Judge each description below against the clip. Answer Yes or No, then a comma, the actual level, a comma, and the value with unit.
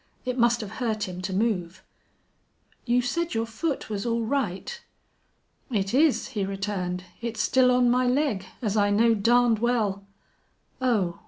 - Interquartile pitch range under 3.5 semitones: No, average, 3.8 semitones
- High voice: Yes, high, 225 Hz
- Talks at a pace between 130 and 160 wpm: Yes, average, 155 wpm